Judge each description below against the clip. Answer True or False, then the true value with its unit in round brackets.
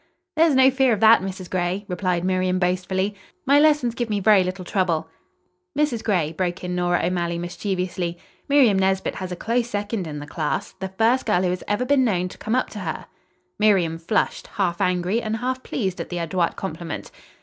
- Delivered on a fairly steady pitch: False (3.9 semitones)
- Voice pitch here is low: False (190 Hz)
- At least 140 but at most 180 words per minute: False (195 wpm)